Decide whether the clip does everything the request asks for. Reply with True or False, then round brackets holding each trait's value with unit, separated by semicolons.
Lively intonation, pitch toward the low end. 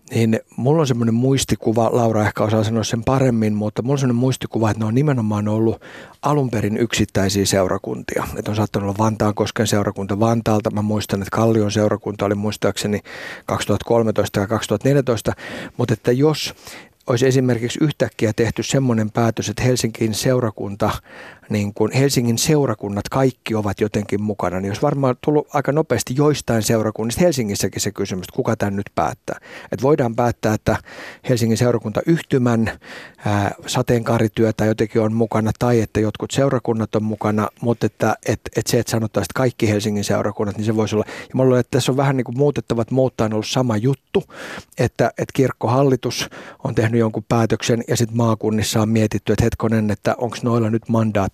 False (2.9 semitones; 115 Hz)